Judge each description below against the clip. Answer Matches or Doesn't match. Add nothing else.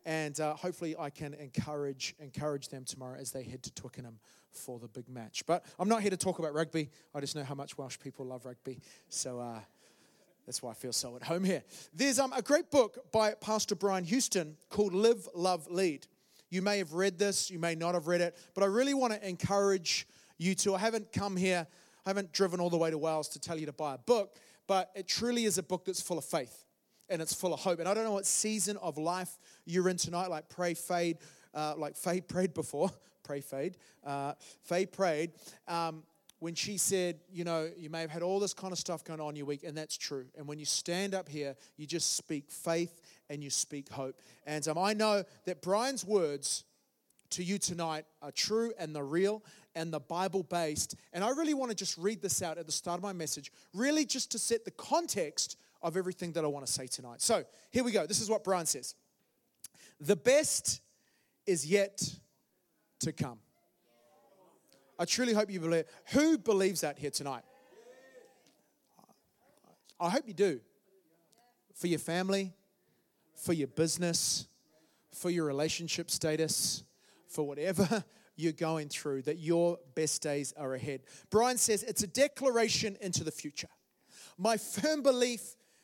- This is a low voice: Doesn't match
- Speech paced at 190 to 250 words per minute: Matches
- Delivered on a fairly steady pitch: Doesn't match